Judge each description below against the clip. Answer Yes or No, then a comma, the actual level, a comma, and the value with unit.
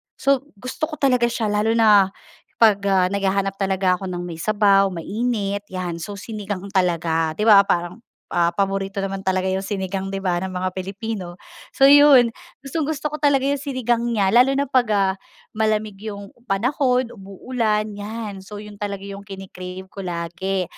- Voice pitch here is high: Yes, high, 200 Hz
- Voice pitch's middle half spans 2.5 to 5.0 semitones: Yes, average, 3.5 semitones